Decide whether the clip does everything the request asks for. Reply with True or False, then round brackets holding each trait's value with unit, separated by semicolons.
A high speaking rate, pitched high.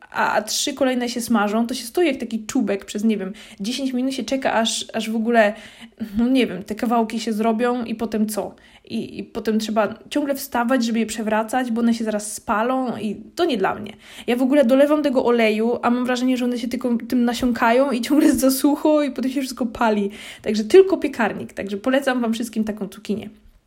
True (210 wpm; 235 Hz)